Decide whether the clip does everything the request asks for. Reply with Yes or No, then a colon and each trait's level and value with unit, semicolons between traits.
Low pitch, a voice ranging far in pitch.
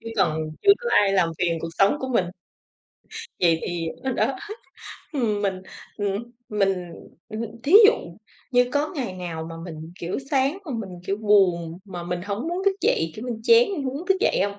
No: high, 205 Hz; wide, 6.7 semitones